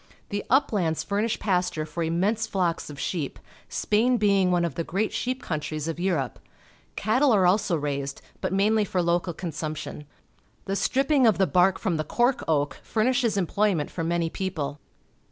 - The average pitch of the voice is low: No, medium, 185 Hz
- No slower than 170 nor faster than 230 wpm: Yes, average, 175 wpm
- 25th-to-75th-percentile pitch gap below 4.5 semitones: No, average, 4.8 semitones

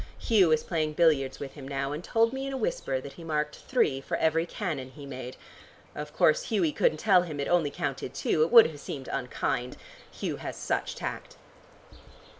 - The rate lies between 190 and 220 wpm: Yes, average, 200 wpm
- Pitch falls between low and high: Yes, medium, 155 Hz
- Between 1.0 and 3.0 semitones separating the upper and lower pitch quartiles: No, average, 4.1 semitones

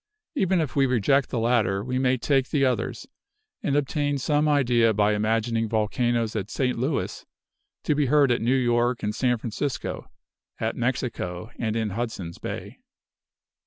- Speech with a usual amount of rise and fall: Yes, average, 3.5 semitones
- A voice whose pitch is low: Yes, low, 120 Hz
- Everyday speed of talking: Yes, average, 160 wpm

